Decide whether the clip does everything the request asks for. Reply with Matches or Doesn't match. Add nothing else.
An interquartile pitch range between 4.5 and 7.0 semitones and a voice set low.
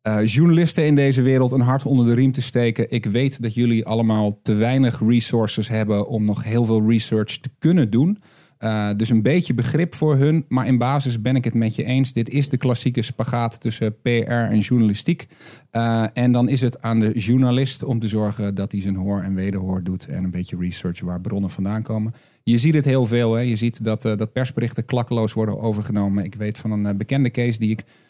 Doesn't match